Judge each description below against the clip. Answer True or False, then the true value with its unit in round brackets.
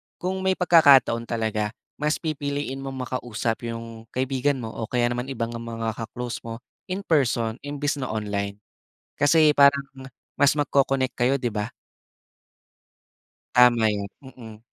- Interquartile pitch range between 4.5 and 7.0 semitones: False (3.7 semitones)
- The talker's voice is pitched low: True (125 Hz)